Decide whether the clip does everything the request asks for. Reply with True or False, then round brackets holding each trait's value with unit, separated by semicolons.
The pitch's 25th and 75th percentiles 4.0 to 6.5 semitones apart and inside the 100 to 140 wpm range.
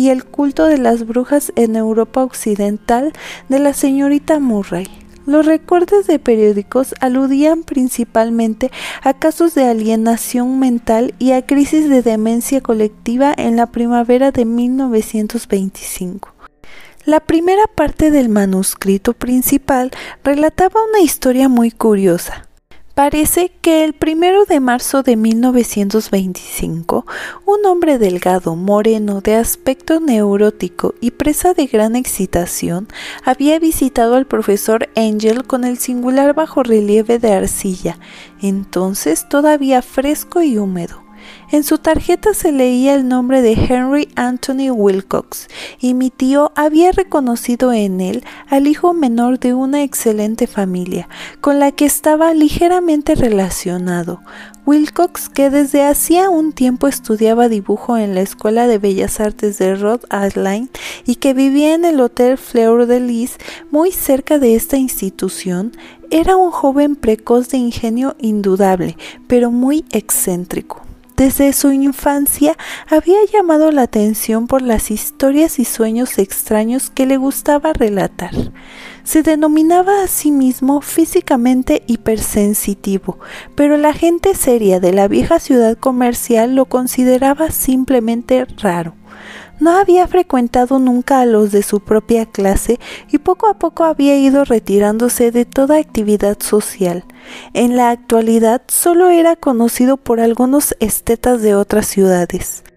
True (4.8 semitones; 130 wpm)